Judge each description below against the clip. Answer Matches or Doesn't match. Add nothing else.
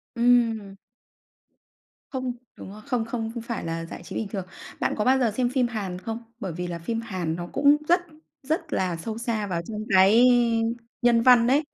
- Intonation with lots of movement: Doesn't match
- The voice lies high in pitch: Matches